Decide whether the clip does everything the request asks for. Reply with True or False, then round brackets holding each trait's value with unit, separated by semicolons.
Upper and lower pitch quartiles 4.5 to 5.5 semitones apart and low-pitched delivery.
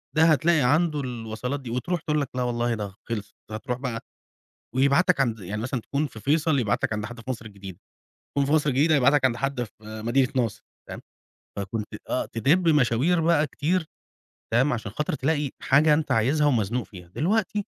True (5.0 semitones; 130 Hz)